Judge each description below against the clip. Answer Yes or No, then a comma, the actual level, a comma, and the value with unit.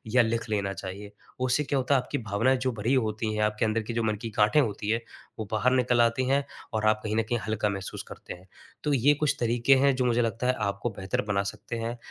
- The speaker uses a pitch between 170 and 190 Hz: No, low, 115 Hz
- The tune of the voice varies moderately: Yes, average, 3.0 semitones